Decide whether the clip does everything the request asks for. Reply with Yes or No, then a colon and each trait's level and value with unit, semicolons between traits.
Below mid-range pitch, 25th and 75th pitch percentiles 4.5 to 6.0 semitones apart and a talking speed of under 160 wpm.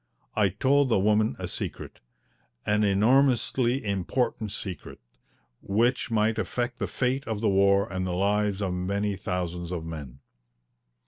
No: low, 105 Hz; average, 3.9 semitones; average, 140 wpm